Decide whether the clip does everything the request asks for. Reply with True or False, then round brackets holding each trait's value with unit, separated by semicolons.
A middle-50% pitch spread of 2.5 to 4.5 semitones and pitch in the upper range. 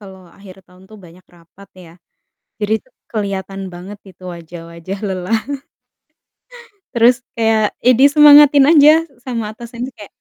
False (4.9 semitones; 210 Hz)